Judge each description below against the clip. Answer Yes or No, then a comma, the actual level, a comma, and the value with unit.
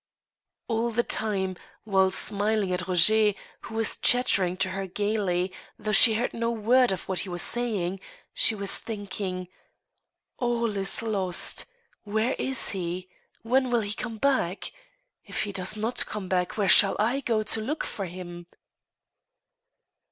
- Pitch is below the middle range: No, high, 210 Hz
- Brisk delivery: No, average, 155 wpm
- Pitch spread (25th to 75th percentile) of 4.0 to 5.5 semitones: No, average, 3.3 semitones